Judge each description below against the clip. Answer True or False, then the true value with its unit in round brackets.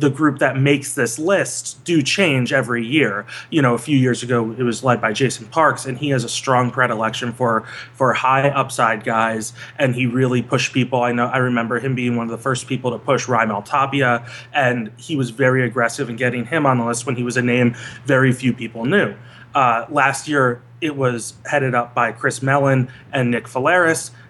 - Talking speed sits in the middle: False (210 wpm)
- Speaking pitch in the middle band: False (125 Hz)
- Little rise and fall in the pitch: True (2.1 semitones)